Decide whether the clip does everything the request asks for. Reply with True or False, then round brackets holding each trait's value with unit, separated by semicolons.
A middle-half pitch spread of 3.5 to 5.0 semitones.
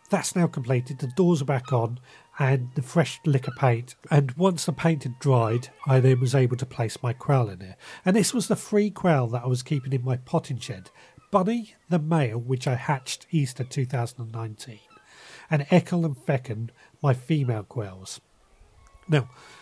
True (4.4 semitones)